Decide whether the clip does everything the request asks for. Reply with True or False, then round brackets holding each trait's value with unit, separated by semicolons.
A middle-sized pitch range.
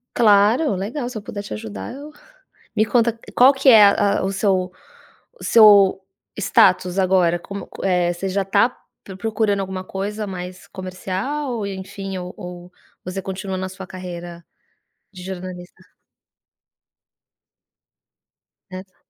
False (2.2 semitones)